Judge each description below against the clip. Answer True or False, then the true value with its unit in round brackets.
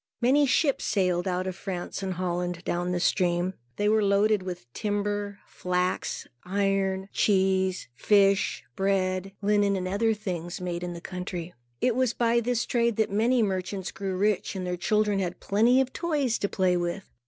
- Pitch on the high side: True (195 Hz)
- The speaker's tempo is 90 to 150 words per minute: False (170 wpm)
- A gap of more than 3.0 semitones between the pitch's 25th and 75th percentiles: False (2.7 semitones)